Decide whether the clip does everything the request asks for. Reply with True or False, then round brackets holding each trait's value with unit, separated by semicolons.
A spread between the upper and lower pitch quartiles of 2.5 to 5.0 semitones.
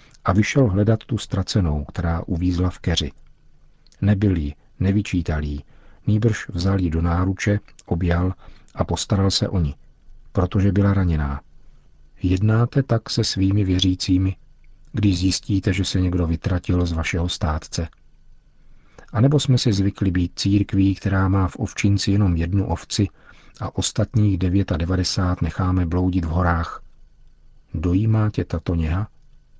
True (2.8 semitones)